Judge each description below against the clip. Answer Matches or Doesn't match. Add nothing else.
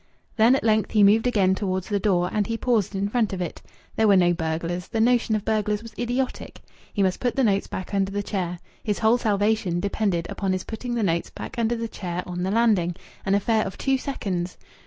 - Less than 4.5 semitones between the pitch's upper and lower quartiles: Matches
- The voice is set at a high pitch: Matches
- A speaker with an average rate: Doesn't match